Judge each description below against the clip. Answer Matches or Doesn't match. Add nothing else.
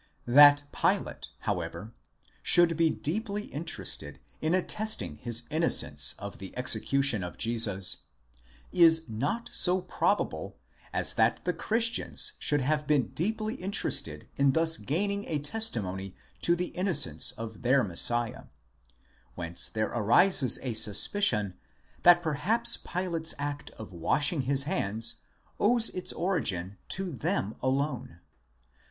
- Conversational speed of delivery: Doesn't match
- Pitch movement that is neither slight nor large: Doesn't match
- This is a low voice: Doesn't match